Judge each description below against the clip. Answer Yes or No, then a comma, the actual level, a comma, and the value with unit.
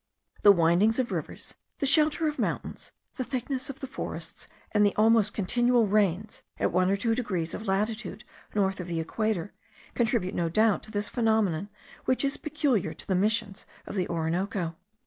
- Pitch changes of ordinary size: Yes, average, 4.4 semitones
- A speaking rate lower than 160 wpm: No, average, 175 wpm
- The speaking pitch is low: No, high, 210 Hz